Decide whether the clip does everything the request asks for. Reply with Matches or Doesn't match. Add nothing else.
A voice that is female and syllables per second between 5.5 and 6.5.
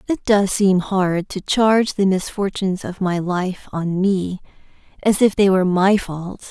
Doesn't match